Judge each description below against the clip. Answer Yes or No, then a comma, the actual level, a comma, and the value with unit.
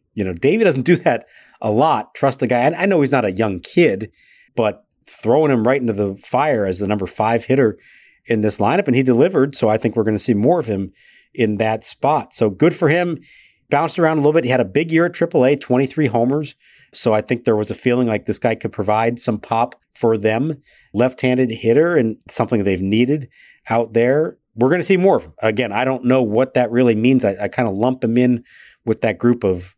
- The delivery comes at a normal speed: No, fast, 240 wpm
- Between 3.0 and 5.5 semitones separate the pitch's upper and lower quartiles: Yes, average, 3.3 semitones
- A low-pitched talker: Yes, low, 120 Hz